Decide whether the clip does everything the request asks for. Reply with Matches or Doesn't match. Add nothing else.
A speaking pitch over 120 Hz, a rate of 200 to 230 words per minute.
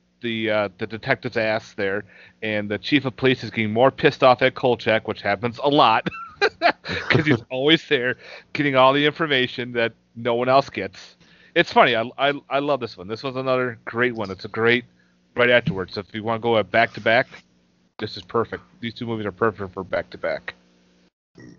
Doesn't match